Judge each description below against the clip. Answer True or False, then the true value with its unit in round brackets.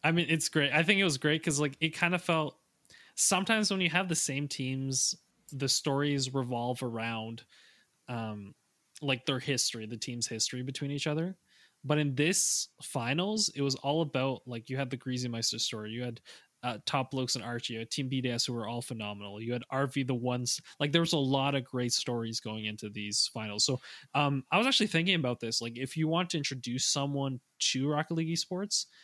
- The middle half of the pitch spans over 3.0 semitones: True (4.6 semitones)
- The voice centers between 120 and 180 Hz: True (135 Hz)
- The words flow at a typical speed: False (210 wpm)